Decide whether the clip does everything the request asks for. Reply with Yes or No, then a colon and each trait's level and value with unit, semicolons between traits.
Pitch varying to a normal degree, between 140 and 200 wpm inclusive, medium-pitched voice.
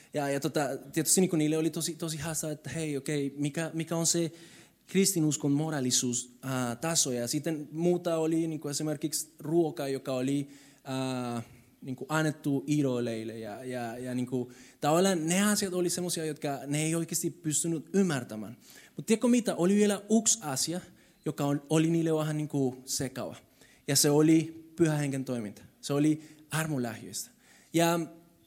Yes: average, 3.6 semitones; average, 150 wpm; medium, 155 Hz